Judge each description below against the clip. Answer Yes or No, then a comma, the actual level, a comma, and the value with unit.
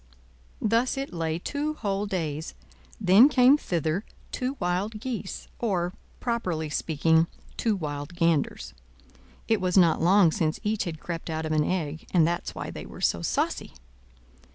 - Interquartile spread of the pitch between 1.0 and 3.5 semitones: No, average, 4.9 semitones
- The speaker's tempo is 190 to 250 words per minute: No, average, 155 wpm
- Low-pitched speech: No, medium, 180 Hz